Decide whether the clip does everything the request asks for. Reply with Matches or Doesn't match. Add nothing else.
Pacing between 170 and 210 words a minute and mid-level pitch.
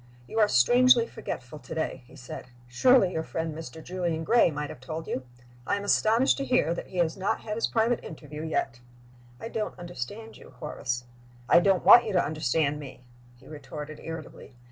Matches